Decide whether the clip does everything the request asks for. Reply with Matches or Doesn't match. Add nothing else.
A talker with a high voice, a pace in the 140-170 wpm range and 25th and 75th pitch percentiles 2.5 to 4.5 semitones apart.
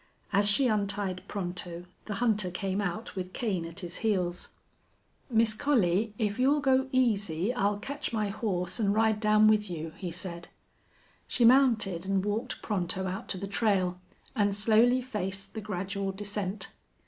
Matches